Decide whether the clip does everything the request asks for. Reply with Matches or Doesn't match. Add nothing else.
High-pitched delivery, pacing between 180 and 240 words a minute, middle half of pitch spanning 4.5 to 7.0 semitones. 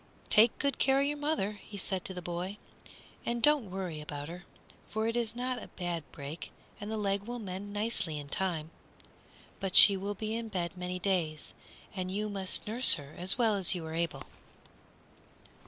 Doesn't match